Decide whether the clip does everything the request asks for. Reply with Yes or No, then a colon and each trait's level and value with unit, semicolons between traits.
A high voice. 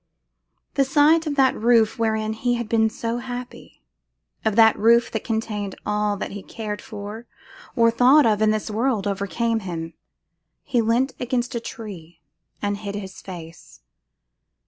Yes: high, 220 Hz